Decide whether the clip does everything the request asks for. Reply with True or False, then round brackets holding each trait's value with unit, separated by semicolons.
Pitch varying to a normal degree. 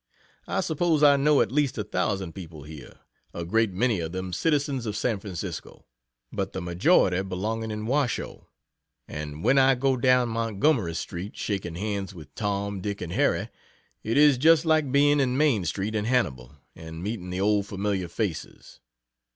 False (6.2 semitones)